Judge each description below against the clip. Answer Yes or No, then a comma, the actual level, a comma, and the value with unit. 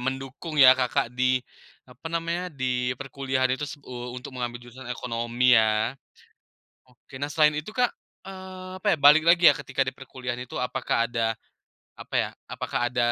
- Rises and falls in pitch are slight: No, average, 3.2 semitones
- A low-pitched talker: Yes, low, 130 Hz